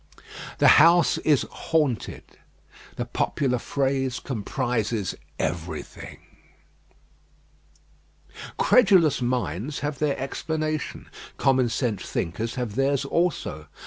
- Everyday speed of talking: No, slow, 85 wpm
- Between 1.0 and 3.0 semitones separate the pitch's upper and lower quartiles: No, average, 4.3 semitones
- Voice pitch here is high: No, low, 135 Hz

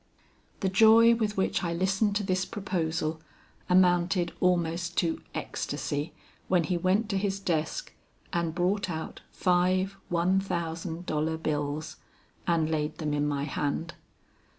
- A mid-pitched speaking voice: Yes, medium, 175 Hz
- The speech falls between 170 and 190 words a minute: No, slow, 135 wpm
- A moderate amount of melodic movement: Yes, average, 3.1 semitones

